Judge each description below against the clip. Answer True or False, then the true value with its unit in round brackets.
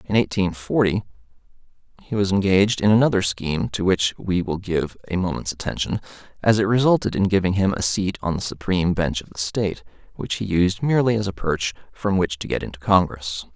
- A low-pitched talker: True (95 Hz)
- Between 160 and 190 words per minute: False (200 wpm)